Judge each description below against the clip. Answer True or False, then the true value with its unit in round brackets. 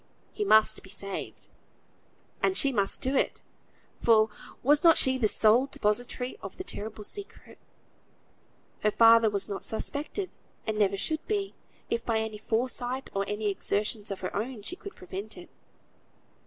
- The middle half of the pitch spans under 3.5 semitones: False (4.4 semitones)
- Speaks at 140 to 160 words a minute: True (155 wpm)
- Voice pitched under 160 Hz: False (225 Hz)